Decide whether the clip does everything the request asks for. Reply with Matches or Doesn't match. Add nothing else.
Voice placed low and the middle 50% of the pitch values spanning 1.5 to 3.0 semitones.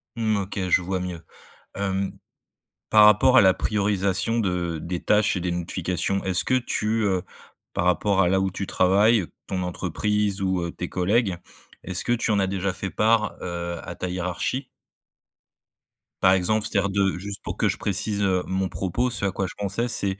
Matches